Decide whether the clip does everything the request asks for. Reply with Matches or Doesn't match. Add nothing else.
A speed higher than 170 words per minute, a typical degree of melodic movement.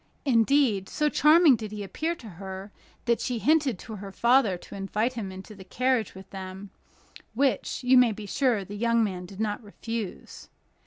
Matches